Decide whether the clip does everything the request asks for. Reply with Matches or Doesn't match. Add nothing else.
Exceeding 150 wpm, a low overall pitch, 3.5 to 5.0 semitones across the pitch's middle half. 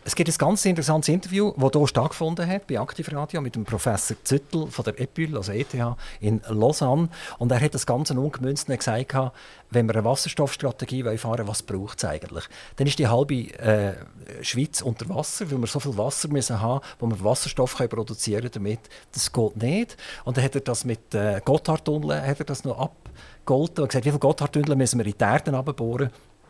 Matches